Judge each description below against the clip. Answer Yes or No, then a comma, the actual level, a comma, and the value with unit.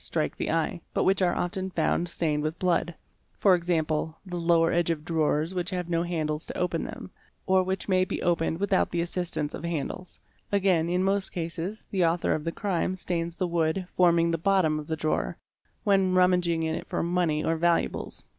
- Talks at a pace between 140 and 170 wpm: No, average, 195 wpm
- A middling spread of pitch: No, narrow, 2.0 semitones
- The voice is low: No, medium, 170 Hz